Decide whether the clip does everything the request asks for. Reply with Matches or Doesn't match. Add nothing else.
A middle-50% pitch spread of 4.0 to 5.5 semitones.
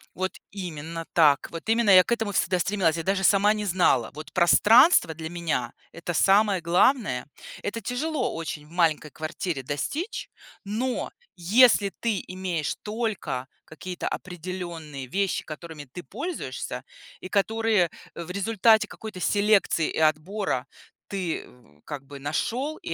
Matches